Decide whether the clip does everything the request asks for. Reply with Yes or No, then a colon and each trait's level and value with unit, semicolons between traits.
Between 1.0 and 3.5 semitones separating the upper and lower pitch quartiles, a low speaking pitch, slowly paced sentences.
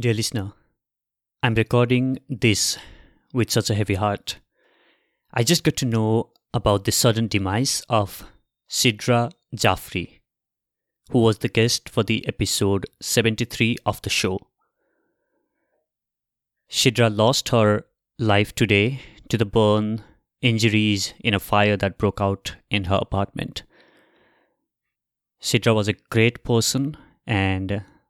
Yes: average, 2.7 semitones; low, 115 Hz; slow, 120 wpm